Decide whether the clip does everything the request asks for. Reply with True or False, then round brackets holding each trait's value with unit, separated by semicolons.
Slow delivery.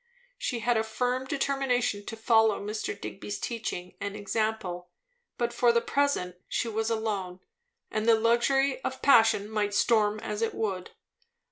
False (150 wpm)